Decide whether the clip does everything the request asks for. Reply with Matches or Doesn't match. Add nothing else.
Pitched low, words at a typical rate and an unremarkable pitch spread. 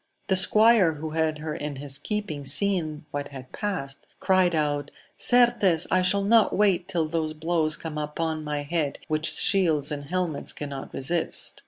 Doesn't match